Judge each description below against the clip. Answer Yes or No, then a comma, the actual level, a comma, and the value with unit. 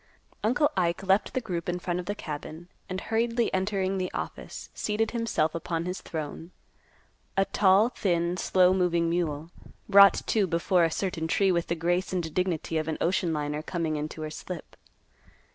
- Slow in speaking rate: No, average, 175 wpm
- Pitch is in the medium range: Yes, medium, 180 Hz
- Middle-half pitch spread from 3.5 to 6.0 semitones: No, average, 2.7 semitones